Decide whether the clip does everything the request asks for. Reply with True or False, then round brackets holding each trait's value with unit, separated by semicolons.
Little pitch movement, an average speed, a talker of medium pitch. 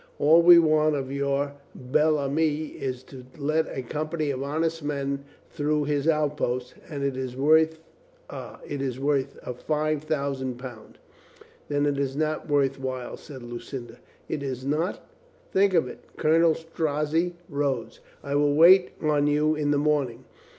True (2.3 semitones; 165 wpm; 145 Hz)